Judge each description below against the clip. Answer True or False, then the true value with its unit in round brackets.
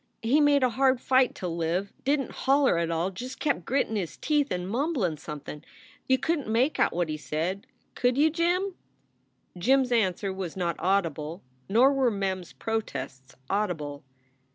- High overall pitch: True (210 Hz)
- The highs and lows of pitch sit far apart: True (7.5 semitones)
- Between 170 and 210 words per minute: True (175 wpm)